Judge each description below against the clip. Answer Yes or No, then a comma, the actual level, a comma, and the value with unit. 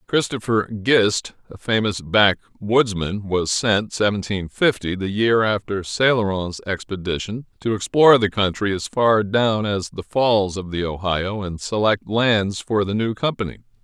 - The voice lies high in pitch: No, low, 105 Hz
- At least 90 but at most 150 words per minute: Yes, average, 145 wpm